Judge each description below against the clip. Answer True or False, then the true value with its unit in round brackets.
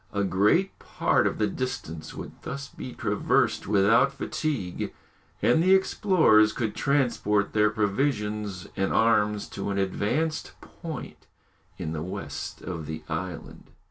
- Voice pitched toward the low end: True (105 Hz)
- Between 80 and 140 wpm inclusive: True (135 wpm)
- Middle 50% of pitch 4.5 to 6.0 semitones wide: True (5.5 semitones)